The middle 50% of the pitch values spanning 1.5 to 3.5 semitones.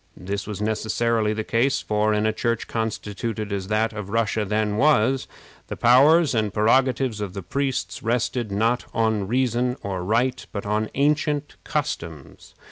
Yes: average, 2.8 semitones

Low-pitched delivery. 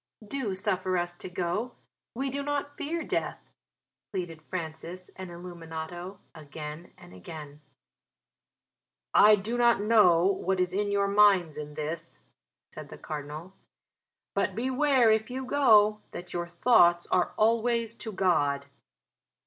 No: medium, 185 Hz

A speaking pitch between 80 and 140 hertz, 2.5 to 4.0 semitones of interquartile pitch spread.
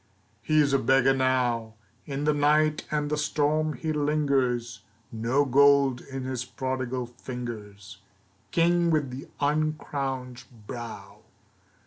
Yes: low, 135 Hz; average, 3.2 semitones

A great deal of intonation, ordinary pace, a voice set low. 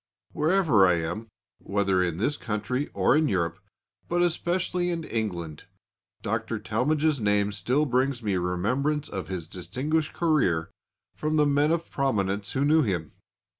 Yes: wide, 7.9 semitones; average, 145 wpm; low, 115 Hz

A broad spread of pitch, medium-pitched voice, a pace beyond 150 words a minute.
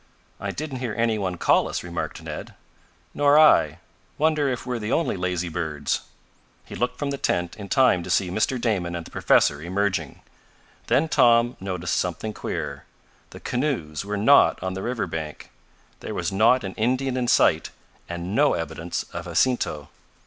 No: wide, 6.4 semitones; low, 100 Hz; average, 170 wpm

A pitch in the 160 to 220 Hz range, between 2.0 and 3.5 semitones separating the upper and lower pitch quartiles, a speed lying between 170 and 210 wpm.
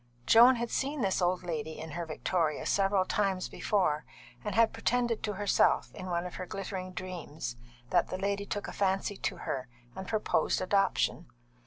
Yes: high, 190 Hz; average, 2.8 semitones; average, 175 wpm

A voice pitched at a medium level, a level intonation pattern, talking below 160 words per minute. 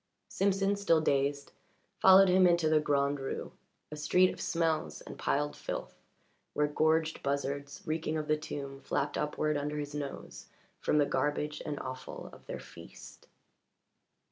Yes: medium, 150 Hz; narrow, 2.1 semitones; average, 150 wpm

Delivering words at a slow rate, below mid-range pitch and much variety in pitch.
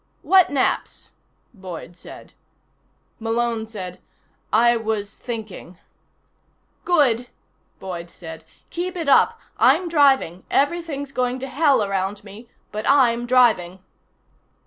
No: slow, 110 wpm; high, 235 Hz; wide, 5.8 semitones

